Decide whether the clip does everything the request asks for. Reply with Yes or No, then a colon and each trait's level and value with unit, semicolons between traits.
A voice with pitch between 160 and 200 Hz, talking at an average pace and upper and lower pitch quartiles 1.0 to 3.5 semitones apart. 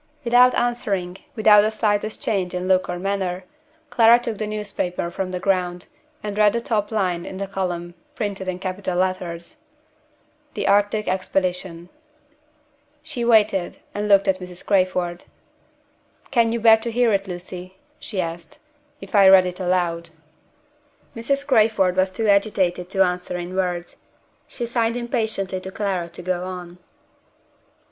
Yes: high, 190 Hz; average, 150 wpm; average, 3.1 semitones